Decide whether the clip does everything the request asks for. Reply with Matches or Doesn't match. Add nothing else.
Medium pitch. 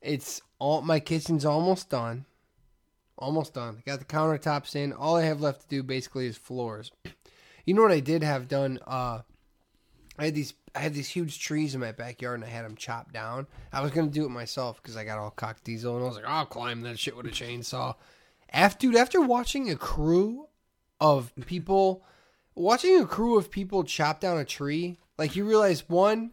Matches